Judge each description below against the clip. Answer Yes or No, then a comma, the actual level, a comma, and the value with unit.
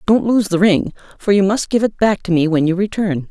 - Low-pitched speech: No, high, 195 Hz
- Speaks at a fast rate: Yes, fast, 270 wpm